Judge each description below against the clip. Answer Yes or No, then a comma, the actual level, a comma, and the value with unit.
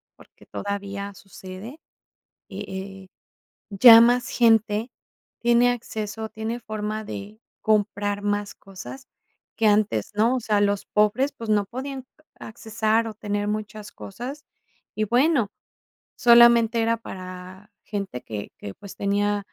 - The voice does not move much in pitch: Yes, narrow, 2.3 semitones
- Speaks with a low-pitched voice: No, high, 215 Hz